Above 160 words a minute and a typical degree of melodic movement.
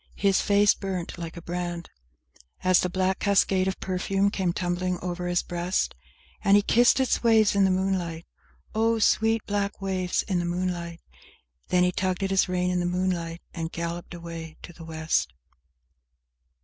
No: average, 170 wpm; narrow, 2.0 semitones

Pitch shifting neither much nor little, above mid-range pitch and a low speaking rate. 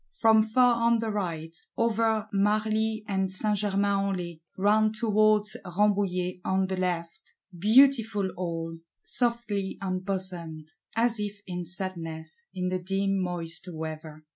Yes: average, 3.3 semitones; high, 195 Hz; slow, 130 wpm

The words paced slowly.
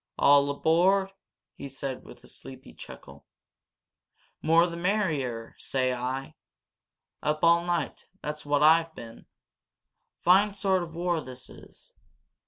Yes: slow, 125 wpm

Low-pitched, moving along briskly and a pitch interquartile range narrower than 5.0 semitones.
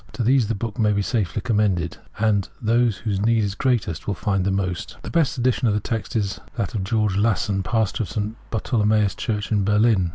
Yes: low, 105 Hz; fast, 215 wpm; narrow, 2.6 semitones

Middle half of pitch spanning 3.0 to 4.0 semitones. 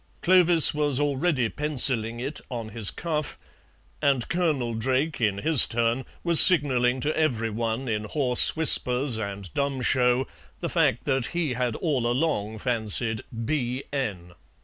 No: average, 4.4 semitones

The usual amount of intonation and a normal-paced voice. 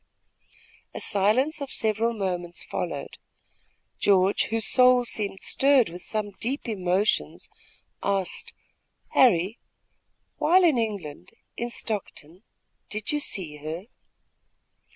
No: average, 4.7 semitones; slow, 105 wpm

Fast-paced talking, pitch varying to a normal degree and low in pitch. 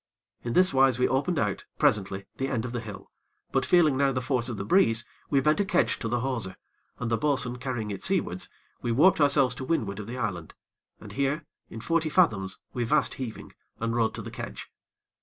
Yes: fast, 215 wpm; average, 4.0 semitones; low, 125 Hz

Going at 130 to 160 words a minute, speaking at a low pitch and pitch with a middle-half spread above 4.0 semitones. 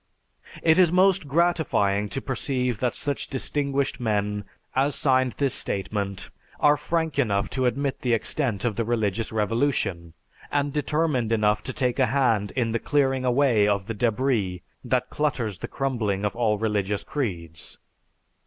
Yes: average, 155 wpm; low, 120 Hz; average, 5.0 semitones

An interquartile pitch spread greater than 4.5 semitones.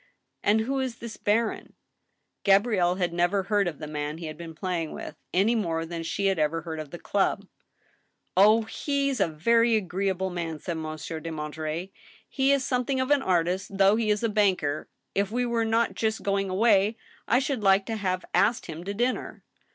Yes: average, 5.0 semitones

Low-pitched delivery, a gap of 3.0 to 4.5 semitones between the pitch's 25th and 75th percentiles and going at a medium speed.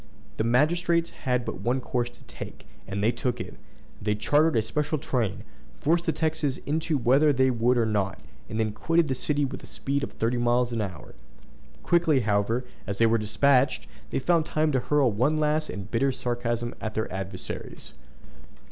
No: low, 125 Hz; average, 4.9 semitones; average, 190 wpm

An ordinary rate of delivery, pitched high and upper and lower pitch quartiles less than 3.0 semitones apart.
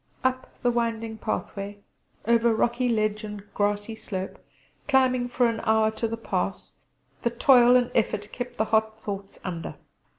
Yes: average, 155 wpm; high, 220 Hz; narrow, 2.6 semitones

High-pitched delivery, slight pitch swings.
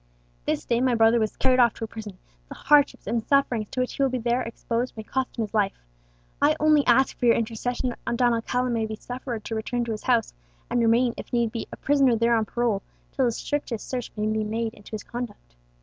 Yes: high, 235 Hz; narrow, 2.2 semitones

